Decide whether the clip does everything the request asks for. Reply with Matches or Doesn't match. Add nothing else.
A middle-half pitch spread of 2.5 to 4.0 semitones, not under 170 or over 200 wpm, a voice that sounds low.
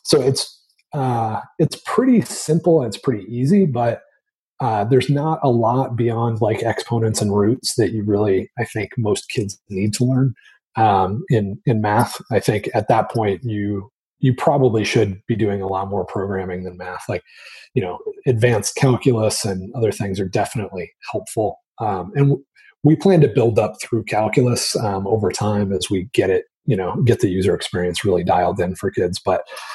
Doesn't match